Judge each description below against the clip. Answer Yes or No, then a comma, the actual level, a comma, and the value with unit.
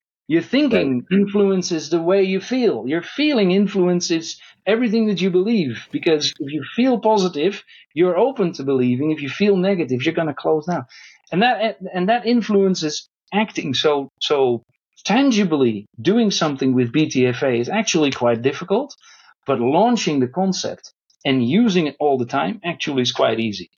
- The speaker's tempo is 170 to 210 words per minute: No, average, 160 wpm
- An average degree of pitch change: No, wide, 6.7 semitones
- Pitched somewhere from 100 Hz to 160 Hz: No, medium, 175 Hz